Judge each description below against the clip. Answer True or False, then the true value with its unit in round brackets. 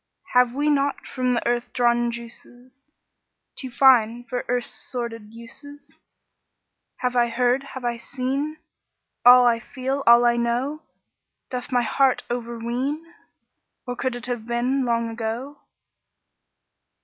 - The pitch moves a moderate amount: False (1.9 semitones)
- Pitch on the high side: True (245 Hz)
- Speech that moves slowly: True (130 wpm)